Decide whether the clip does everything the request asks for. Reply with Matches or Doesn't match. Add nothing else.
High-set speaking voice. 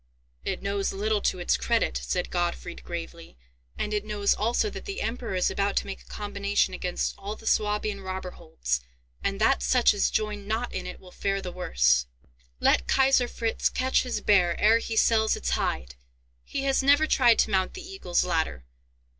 Matches